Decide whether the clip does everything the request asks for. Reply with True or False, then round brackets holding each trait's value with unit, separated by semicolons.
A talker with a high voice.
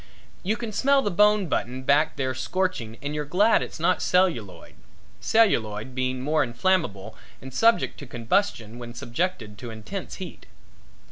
False (145 Hz)